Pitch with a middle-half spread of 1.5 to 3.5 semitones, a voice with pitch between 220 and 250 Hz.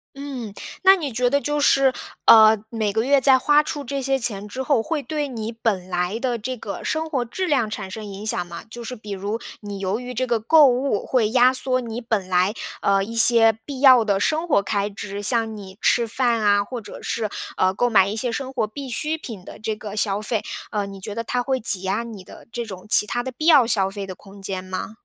No: average, 4.2 semitones; high, 225 Hz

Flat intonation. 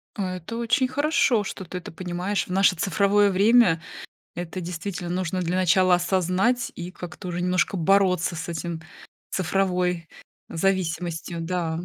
Yes: narrow, 2.2 semitones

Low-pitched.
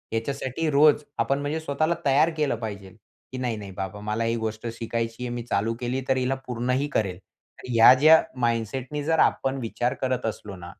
Yes: low, 125 Hz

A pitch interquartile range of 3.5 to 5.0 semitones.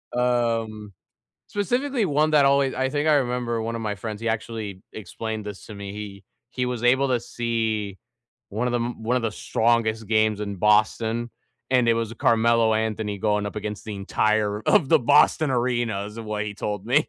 No: average, 2.7 semitones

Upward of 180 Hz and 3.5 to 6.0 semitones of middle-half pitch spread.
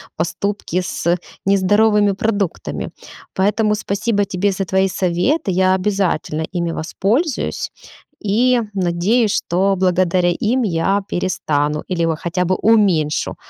No: high, 190 Hz; average, 3.0 semitones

